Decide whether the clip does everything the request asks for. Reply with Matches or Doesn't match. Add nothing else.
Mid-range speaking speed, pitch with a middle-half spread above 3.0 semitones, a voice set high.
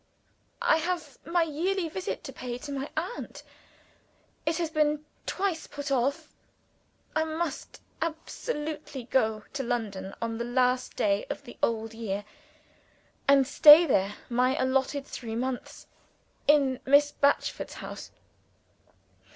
Doesn't match